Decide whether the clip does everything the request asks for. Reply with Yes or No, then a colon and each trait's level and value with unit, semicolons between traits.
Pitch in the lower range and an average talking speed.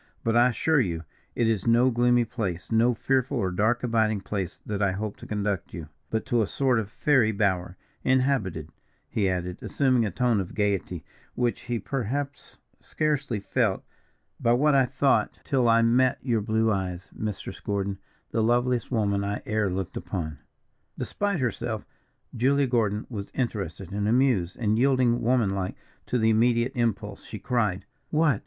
Yes: low, 115 Hz; average, 165 wpm